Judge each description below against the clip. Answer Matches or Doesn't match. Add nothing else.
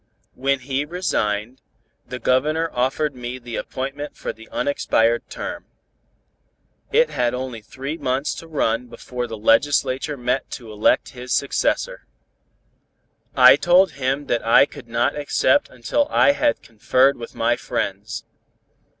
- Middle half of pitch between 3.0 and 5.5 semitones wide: Matches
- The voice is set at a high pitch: Doesn't match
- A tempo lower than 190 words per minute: Matches